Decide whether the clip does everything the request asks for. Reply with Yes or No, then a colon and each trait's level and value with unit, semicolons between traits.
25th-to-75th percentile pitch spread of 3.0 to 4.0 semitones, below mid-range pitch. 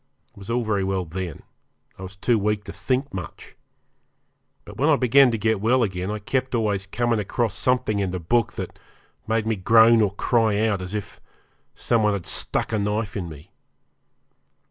Yes: average, 3.3 semitones; low, 105 Hz